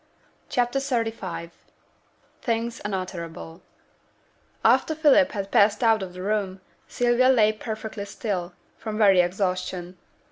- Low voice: No, high, 210 Hz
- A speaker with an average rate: No, slow, 110 wpm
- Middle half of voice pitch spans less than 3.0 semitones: No, average, 4.0 semitones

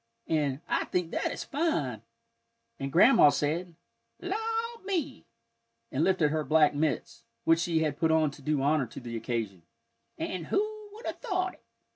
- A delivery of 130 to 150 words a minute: No, average, 165 wpm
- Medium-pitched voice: Yes, medium, 160 Hz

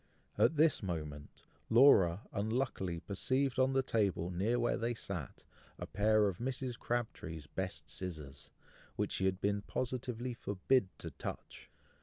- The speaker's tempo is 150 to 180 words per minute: No, average, 140 wpm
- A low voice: Yes, low, 105 Hz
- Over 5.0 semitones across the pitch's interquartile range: Yes, wide, 5.5 semitones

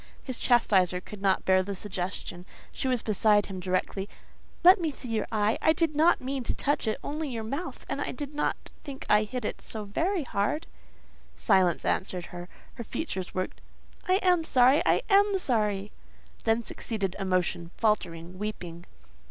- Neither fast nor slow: Yes, average, 165 wpm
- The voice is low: No, high, 215 Hz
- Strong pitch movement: Yes, wide, 6.8 semitones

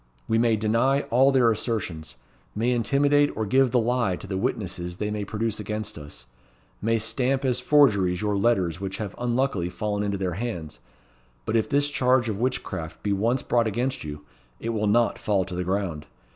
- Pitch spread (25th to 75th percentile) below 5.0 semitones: Yes, average, 4.2 semitones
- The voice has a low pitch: Yes, low, 110 Hz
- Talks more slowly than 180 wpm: No, average, 185 wpm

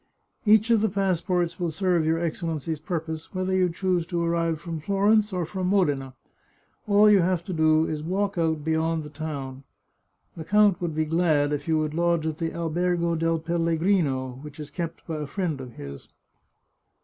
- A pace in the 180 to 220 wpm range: Yes, average, 185 wpm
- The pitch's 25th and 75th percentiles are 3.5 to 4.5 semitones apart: No, average, 2.7 semitones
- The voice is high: No, medium, 165 Hz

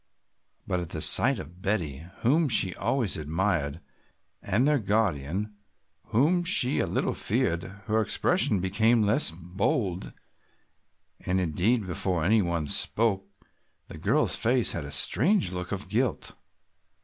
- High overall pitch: No, low, 100 Hz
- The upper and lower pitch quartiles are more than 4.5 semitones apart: Yes, average, 5.0 semitones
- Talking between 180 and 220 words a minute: No, slow, 135 wpm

